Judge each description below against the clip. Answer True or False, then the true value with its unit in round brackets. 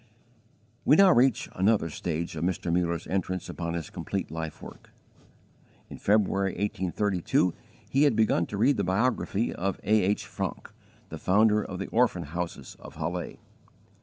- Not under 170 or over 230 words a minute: False (155 wpm)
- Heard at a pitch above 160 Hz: False (95 Hz)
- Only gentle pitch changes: False (3.9 semitones)